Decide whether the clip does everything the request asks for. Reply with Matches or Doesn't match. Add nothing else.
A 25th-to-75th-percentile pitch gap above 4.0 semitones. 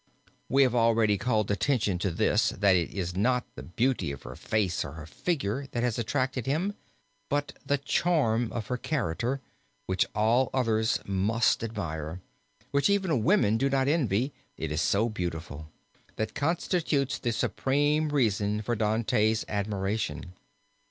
Matches